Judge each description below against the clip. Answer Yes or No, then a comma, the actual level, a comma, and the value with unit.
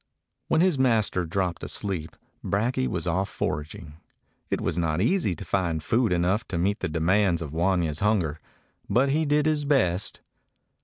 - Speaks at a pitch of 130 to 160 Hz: No, very low, 95 Hz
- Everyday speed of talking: Yes, average, 160 wpm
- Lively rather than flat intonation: Yes, wide, 6.0 semitones